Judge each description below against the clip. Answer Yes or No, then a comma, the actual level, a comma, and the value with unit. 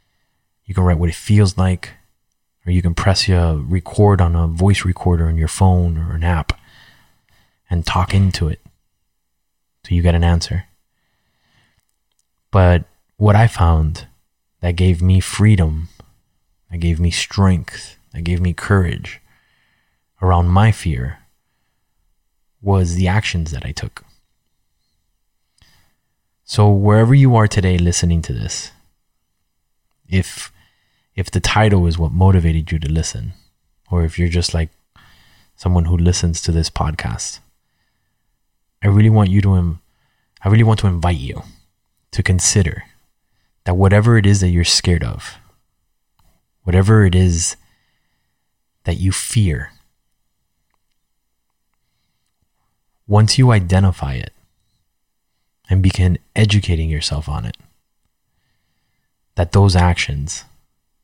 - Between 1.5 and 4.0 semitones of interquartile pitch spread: Yes, average, 3.1 semitones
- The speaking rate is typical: No, slow, 125 wpm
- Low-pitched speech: Yes, very low, 90 Hz